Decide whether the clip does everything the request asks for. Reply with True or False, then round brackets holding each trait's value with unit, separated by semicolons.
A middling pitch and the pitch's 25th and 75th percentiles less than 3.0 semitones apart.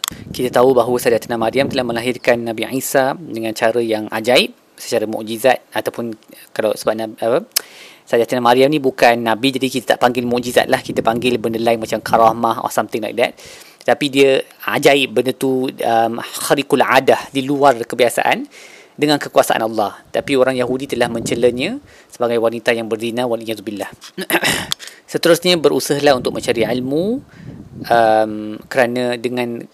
False (125 Hz; 2.5 semitones)